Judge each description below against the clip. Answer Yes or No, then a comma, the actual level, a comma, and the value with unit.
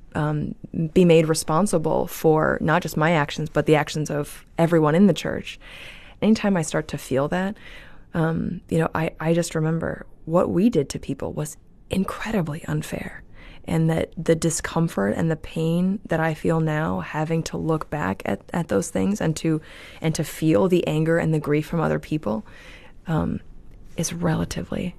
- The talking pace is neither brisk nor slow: Yes, average, 175 wpm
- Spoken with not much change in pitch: Yes, narrow, 1.8 semitones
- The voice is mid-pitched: Yes, medium, 160 Hz